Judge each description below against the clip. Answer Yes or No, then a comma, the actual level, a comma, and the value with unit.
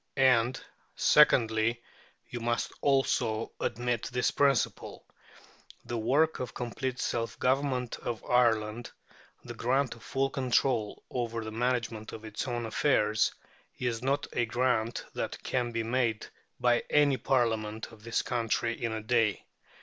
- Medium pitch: No, low, 120 Hz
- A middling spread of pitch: No, narrow, 2.2 semitones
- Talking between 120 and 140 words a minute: Yes, slow, 135 wpm